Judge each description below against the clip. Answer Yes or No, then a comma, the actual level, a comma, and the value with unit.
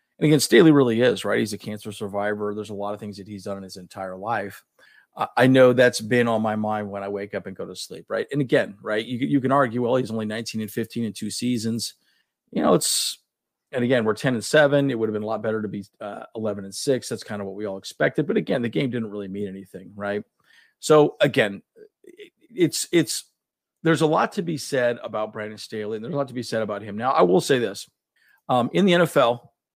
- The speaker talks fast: Yes, fast, 245 wpm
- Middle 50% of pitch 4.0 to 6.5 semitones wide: Yes, average, 5.1 semitones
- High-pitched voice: No, low, 110 Hz